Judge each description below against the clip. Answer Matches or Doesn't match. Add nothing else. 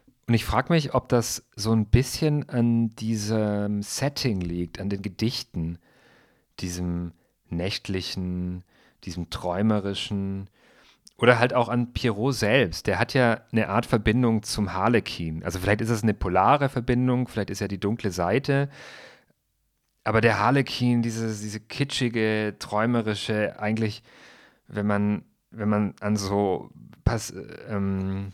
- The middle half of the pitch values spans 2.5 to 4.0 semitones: Matches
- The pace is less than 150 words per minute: Matches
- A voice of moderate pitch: Doesn't match